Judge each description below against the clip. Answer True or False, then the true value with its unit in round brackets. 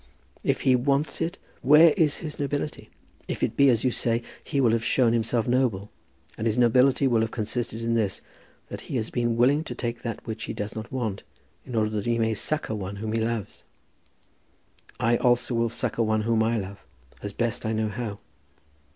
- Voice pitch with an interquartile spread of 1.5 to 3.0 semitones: True (2.5 semitones)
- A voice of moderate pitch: False (115 Hz)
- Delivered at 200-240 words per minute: True (205 wpm)